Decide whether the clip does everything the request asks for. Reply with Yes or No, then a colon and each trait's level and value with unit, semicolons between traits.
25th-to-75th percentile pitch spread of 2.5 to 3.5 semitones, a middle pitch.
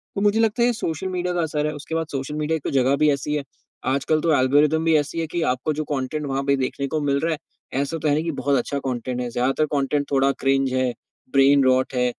Yes: average, 2.9 semitones; medium, 145 Hz